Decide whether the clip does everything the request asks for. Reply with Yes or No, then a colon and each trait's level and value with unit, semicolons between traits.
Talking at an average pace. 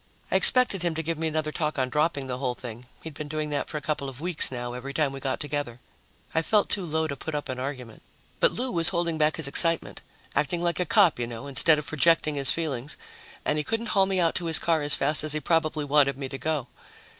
No: fast, 255 wpm